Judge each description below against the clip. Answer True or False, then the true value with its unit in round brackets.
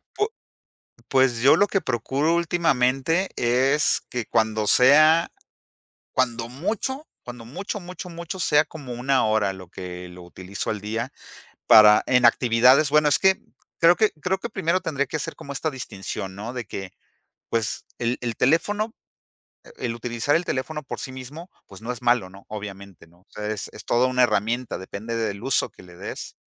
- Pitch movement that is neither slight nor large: False (6.1 semitones)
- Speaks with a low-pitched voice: True (125 Hz)